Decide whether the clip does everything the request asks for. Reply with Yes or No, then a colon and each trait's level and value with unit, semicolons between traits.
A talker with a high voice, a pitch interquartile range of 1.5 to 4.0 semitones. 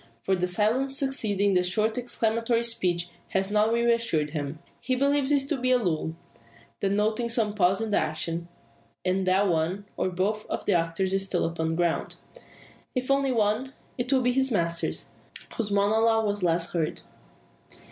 No: high, 210 Hz; average, 4.7 semitones